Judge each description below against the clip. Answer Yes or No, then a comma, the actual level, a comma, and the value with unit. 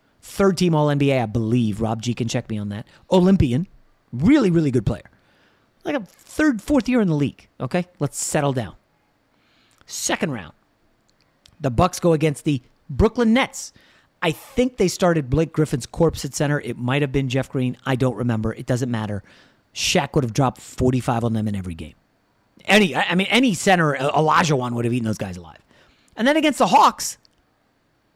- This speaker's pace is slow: No, average, 190 wpm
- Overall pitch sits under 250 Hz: Yes, medium, 140 Hz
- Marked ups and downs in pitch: Yes, wide, 6.9 semitones